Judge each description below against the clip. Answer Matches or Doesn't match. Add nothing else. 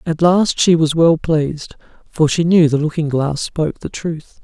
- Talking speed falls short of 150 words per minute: Doesn't match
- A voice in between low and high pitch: Matches